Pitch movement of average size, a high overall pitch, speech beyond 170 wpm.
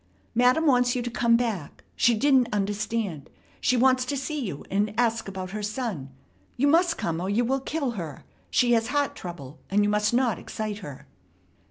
Yes: average, 4.2 semitones; high, 230 Hz; average, 190 wpm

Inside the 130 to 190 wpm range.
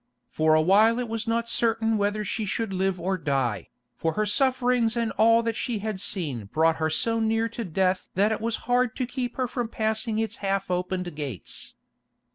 No: average, 200 wpm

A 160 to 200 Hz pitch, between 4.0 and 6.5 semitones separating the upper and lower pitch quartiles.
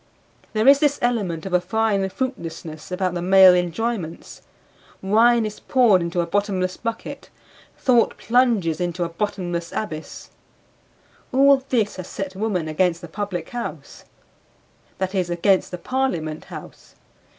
Yes: high, 190 Hz; average, 4.4 semitones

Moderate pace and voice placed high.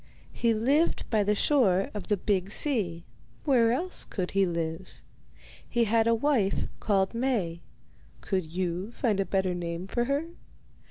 Yes: average, 155 wpm; high, 205 Hz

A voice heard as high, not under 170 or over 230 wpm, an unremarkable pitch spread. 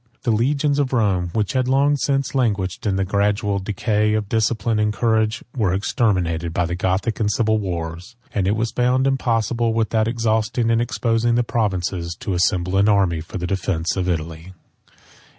No: low, 105 Hz; average, 175 wpm; average, 3.9 semitones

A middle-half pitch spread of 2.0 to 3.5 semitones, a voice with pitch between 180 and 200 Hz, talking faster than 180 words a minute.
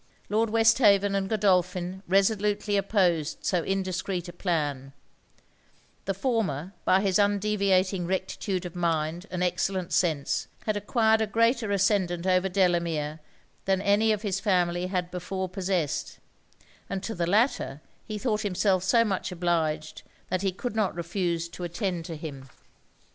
No: average, 2.7 semitones; medium, 185 Hz; average, 145 wpm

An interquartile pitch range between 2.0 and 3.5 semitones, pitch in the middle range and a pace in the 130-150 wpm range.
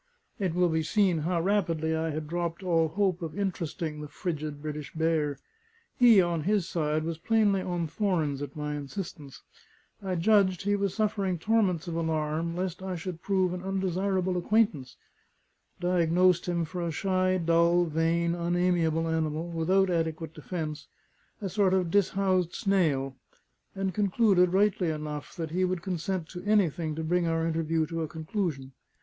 No: average, 2.8 semitones; medium, 170 Hz; average, 160 wpm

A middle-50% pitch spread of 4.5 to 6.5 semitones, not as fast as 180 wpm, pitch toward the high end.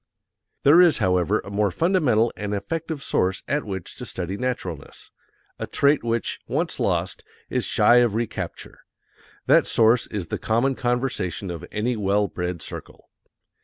No: average, 5.0 semitones; average, 150 wpm; low, 110 Hz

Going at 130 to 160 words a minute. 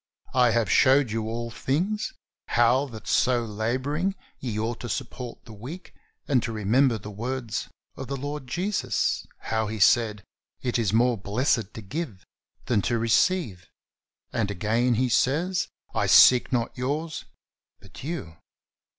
Yes: average, 150 wpm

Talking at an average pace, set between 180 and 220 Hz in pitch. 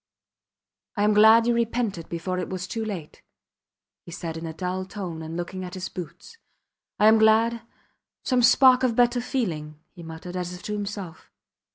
Yes: average, 180 wpm; high, 190 Hz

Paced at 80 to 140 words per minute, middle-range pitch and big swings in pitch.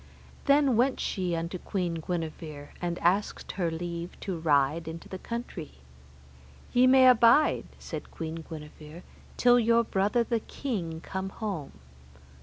Yes: slow, 135 wpm; medium, 175 Hz; wide, 5.9 semitones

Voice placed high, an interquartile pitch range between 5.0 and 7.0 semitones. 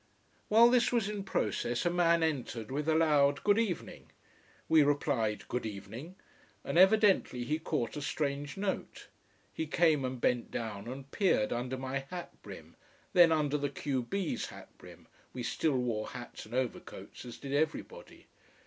No: medium, 145 Hz; wide, 5.6 semitones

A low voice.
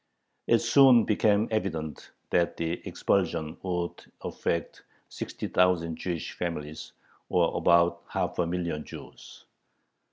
Yes: very low, 85 Hz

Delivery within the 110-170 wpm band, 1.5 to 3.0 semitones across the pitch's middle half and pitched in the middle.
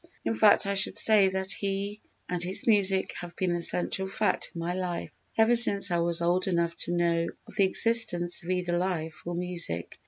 No: fast, 205 wpm; narrow, 2.4 semitones; medium, 180 Hz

